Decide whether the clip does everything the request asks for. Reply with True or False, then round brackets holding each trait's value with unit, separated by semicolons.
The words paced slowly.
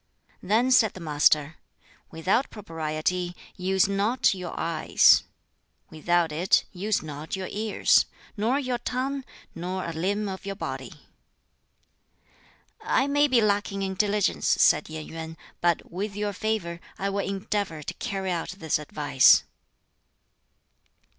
True (130 wpm)